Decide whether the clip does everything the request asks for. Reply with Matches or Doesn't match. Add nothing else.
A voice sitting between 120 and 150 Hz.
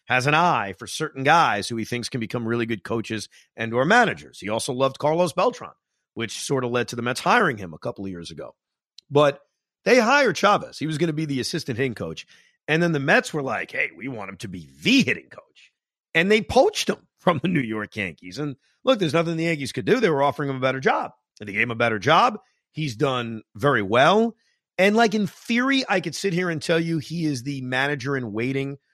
Matches